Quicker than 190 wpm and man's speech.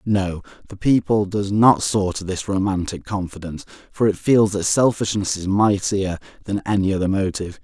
No: average, 165 wpm; male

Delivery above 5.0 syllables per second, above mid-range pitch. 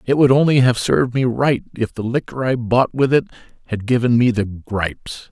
No: 5.2 syllables/s; low, 120 Hz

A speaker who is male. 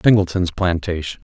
Yes: male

